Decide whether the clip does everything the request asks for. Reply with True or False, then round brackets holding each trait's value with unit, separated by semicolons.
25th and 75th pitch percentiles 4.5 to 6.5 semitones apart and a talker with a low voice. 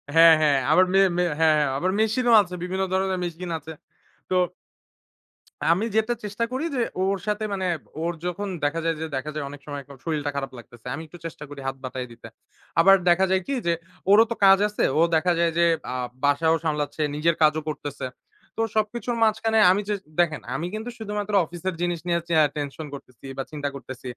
False (4.9 semitones; 170 Hz)